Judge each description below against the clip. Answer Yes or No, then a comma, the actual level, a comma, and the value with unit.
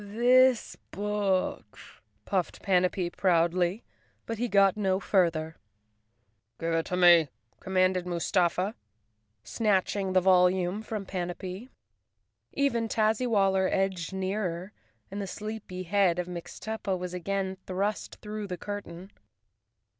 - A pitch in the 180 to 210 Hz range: Yes, high, 190 Hz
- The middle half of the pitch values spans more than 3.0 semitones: No, narrow, 2.6 semitones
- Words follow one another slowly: Yes, slow, 110 wpm